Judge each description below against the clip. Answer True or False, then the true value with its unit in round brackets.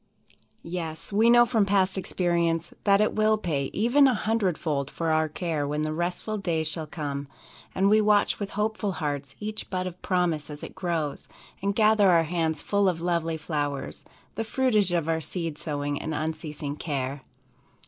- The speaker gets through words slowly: False (180 wpm)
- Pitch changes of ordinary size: True (4.6 semitones)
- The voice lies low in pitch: False (170 Hz)